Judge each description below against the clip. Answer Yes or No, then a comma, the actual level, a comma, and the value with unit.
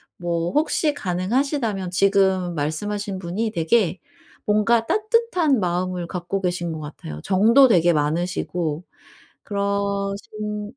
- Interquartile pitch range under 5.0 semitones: Yes, average, 3.4 semitones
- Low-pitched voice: No, high, 195 Hz